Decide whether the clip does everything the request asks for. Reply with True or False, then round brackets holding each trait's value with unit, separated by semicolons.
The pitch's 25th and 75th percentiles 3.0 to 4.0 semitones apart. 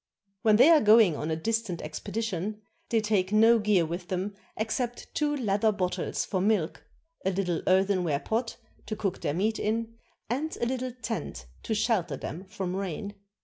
True (3.6 semitones)